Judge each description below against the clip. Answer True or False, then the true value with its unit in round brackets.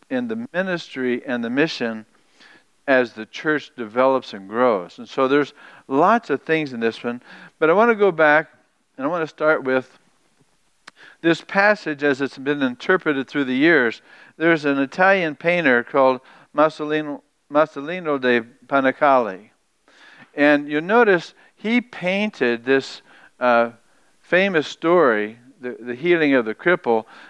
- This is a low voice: False (145 Hz)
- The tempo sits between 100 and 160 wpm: True (145 wpm)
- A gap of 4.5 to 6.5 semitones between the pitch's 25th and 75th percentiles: True (5.3 semitones)